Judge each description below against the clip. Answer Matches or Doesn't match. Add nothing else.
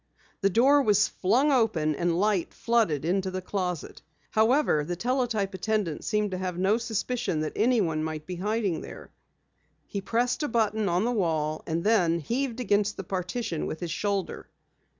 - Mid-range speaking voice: Doesn't match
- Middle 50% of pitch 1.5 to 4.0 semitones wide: Doesn't match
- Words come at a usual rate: Matches